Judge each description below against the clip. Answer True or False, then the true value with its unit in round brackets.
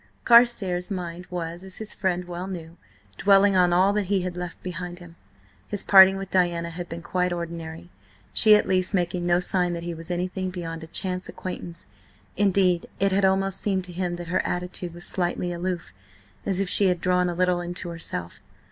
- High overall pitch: False (180 Hz)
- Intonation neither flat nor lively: False (1.5 semitones)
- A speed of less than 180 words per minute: False (195 wpm)